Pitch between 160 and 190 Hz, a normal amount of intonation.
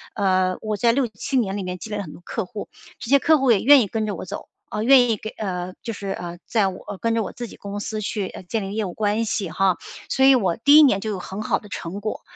No: high, 210 Hz; average, 3.2 semitones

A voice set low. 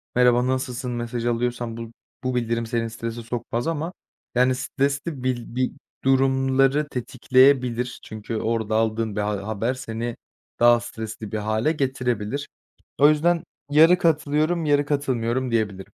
Yes: low, 125 Hz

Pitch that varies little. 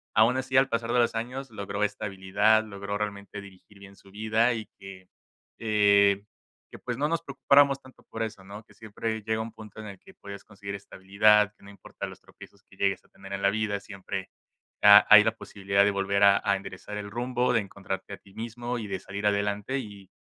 Yes: narrow, 2.2 semitones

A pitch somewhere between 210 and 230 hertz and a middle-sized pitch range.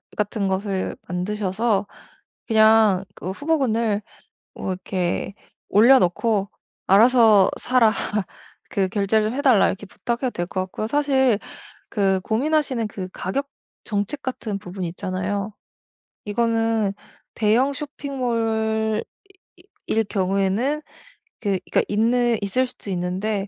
Yes: high, 215 Hz; average, 3.5 semitones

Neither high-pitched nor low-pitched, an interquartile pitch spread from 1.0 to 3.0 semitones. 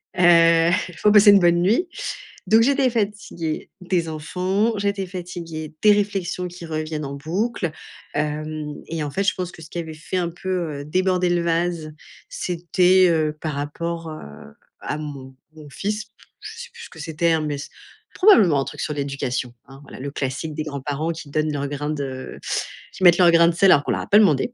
No: medium, 170 Hz; average, 3.5 semitones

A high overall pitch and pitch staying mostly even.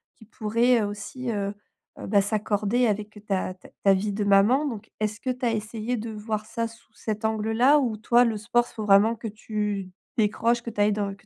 Yes: high, 215 Hz; narrow, 2.1 semitones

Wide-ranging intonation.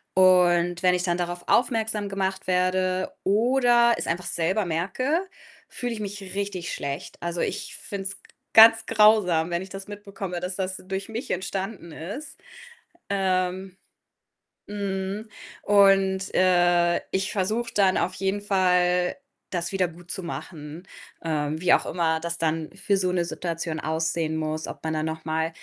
No: narrow, 2.6 semitones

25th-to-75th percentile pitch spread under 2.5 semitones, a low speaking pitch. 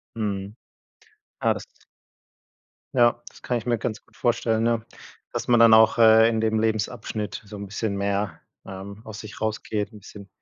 Yes: narrow, 1.9 semitones; low, 110 Hz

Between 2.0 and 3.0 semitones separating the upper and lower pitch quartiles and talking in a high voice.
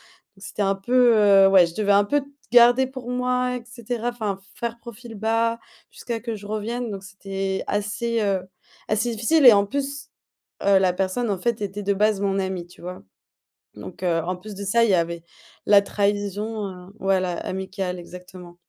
No: average, 3.4 semitones; high, 205 Hz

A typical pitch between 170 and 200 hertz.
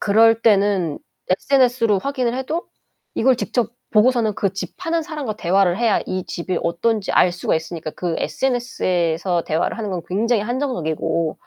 No: high, 210 Hz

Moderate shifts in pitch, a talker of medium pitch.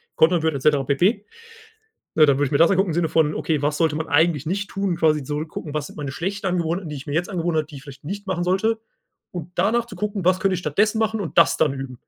Yes: average, 4.3 semitones; medium, 165 Hz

